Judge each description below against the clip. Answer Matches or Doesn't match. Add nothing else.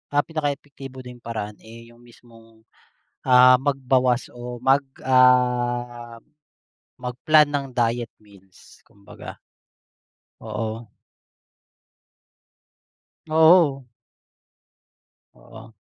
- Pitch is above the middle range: Doesn't match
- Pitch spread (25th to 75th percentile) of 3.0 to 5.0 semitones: Doesn't match